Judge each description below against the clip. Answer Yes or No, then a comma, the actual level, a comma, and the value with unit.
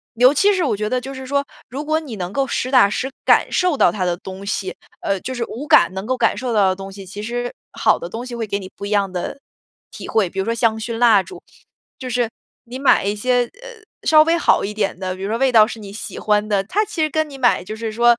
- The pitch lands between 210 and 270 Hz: Yes, high, 230 Hz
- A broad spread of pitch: No, average, 4.8 semitones